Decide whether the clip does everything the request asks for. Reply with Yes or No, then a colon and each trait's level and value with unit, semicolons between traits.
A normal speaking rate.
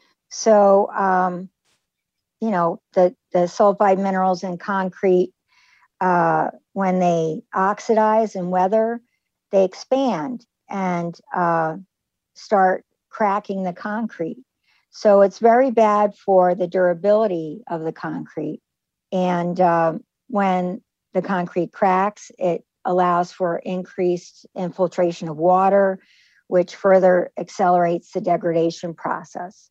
No: slow, 105 wpm